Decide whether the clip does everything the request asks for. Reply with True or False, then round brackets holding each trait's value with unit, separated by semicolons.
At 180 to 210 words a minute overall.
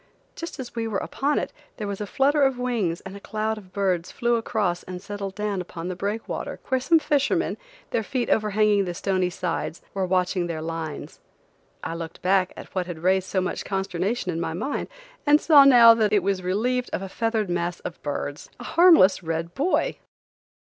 True (195 wpm)